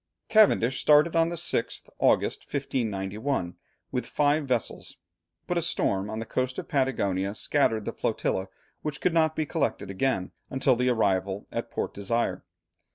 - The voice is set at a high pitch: No, low, 125 Hz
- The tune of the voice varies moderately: No, wide, 6.6 semitones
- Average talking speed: Yes, average, 155 wpm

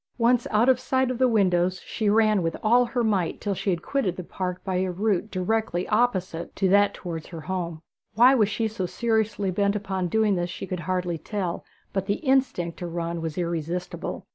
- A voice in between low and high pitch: No, high, 195 Hz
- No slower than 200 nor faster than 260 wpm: Yes, fast, 205 wpm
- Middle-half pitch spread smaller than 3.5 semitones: No, average, 3.8 semitones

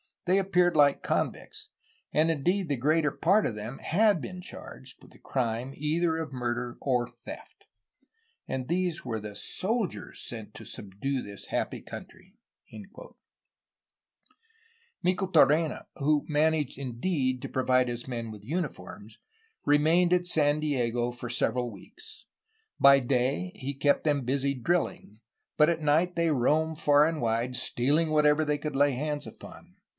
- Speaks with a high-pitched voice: No, medium, 145 Hz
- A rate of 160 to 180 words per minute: No, average, 145 wpm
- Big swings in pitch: No, average, 4.5 semitones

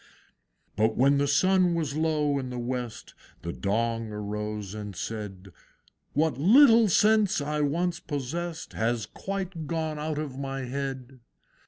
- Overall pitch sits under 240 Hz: Yes, medium, 140 Hz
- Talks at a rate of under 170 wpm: Yes, average, 140 wpm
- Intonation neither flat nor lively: No, wide, 6.0 semitones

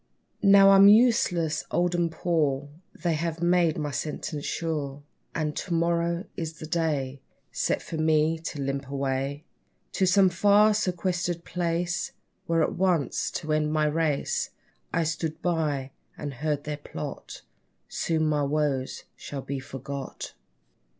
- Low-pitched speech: No, medium, 160 Hz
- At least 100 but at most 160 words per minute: Yes, average, 140 wpm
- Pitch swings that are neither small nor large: Yes, average, 3.0 semitones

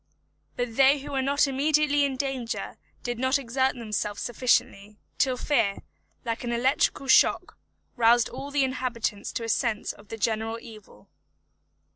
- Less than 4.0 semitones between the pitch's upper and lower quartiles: Yes, average, 3.1 semitones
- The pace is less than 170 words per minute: Yes, average, 150 wpm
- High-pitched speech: Yes, high, 245 Hz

